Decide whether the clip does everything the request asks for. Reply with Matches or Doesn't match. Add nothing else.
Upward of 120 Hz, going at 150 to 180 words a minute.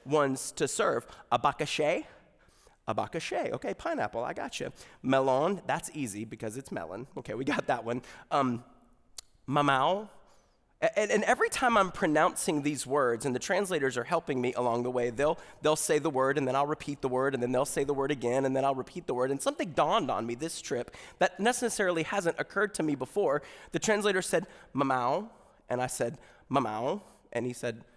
Doesn't match